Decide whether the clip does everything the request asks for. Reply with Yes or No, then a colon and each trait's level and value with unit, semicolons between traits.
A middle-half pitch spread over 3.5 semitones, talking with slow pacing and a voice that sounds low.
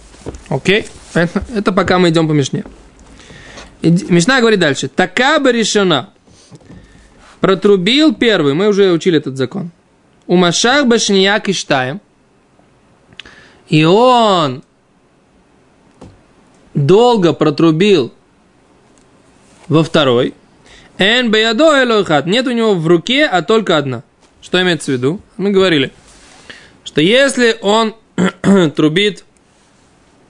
No: average, 5.2 semitones; slow, 105 wpm; high, 190 Hz